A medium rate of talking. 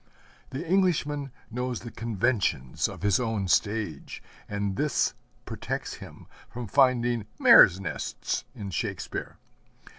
No: slow, 115 wpm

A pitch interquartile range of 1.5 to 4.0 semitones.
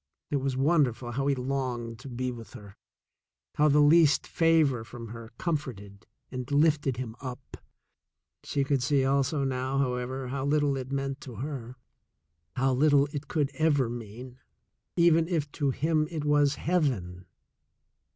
Yes: average, 2.9 semitones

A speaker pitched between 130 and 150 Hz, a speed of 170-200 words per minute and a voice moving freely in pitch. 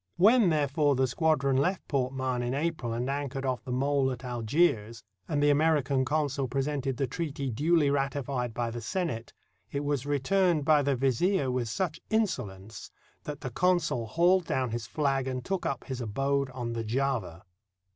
No: low, 135 Hz; average, 175 wpm; average, 3.2 semitones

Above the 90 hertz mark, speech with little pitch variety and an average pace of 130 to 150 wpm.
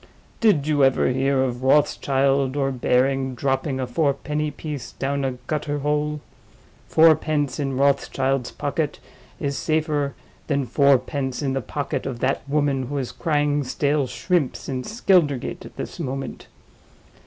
Yes: medium, 140 Hz; narrow, 1.9 semitones; average, 140 wpm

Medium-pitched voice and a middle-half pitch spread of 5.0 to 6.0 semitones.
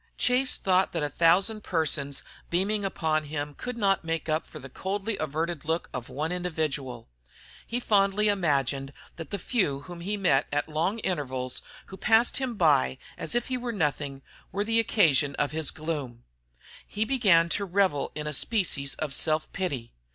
Yes: medium, 165 Hz; wide, 5.6 semitones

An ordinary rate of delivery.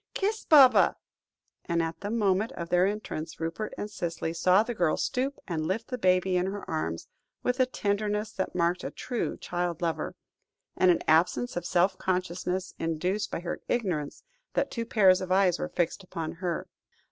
Yes: average, 180 wpm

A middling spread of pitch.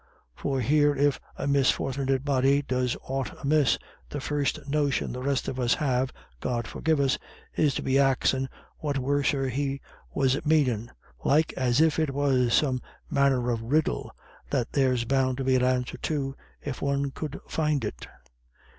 No: narrow, 1.9 semitones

